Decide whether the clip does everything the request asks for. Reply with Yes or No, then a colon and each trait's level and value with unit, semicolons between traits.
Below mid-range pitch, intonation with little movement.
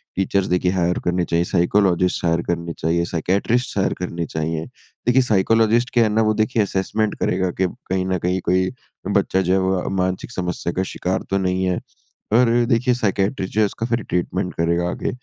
No: very low, 95 Hz; average, 3.3 semitones